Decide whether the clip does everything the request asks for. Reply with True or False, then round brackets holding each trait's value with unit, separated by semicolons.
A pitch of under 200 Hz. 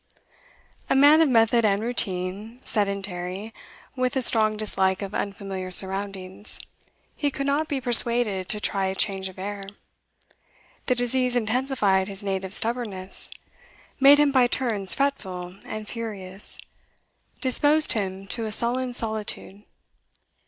False (215 Hz)